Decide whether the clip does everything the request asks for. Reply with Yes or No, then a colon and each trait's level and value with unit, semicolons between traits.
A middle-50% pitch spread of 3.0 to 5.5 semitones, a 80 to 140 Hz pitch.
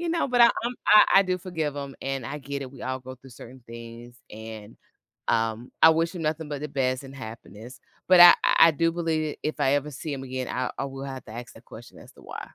Yes: average, 4.1 semitones; low, 135 Hz